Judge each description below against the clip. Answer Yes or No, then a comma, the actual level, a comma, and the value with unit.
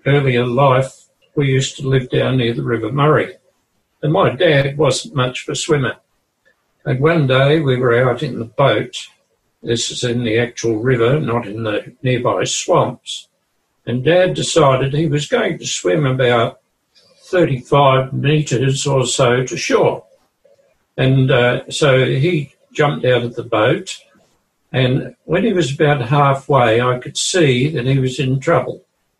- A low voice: Yes, low, 130 Hz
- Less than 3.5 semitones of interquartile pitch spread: Yes, average, 3.0 semitones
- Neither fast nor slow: Yes, average, 160 wpm